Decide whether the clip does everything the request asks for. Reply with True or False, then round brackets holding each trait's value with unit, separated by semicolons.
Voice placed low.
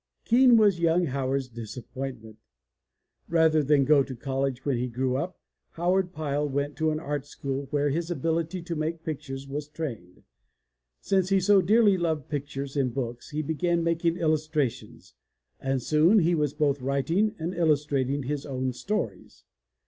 False (150 Hz)